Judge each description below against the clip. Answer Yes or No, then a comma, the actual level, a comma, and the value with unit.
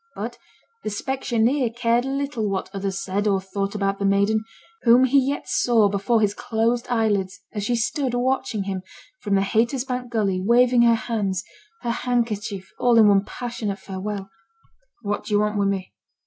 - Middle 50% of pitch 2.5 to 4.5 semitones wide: Yes, average, 3.5 semitones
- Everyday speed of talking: Yes, average, 170 wpm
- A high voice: Yes, high, 220 Hz